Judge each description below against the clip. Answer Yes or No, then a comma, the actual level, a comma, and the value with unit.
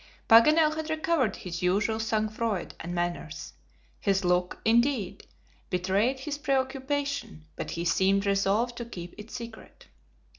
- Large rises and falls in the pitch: Yes, wide, 6.1 semitones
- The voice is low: No, high, 220 Hz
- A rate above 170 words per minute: No, slow, 135 wpm